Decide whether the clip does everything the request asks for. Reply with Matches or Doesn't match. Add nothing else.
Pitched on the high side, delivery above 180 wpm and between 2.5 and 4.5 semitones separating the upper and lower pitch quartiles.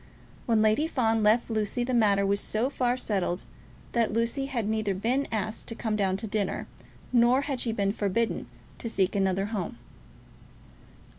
Doesn't match